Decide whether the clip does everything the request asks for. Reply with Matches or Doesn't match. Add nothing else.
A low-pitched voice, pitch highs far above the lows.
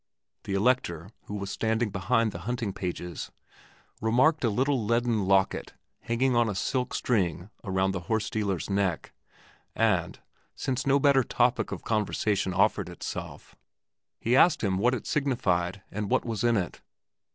Doesn't match